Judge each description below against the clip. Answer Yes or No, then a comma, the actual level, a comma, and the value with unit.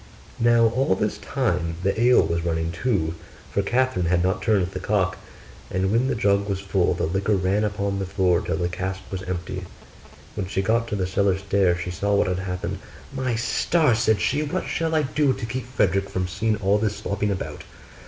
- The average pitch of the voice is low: Yes, low, 100 Hz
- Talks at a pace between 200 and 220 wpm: Yes, fast, 205 wpm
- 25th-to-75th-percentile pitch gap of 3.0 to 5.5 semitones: Yes, average, 3.5 semitones